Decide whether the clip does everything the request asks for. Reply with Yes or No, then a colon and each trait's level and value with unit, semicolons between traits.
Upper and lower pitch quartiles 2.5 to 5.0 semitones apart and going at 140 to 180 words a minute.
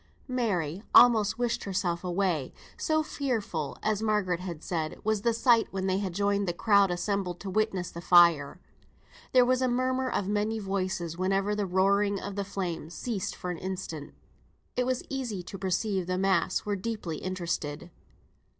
Yes: average, 3.4 semitones; average, 165 wpm